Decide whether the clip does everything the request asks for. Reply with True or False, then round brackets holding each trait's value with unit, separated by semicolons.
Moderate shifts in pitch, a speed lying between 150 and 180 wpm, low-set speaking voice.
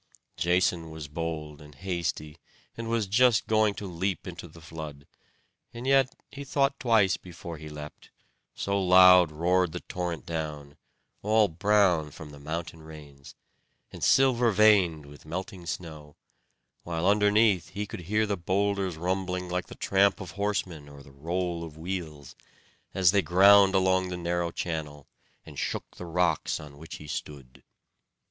True (4.0 semitones; 155 wpm; 90 Hz)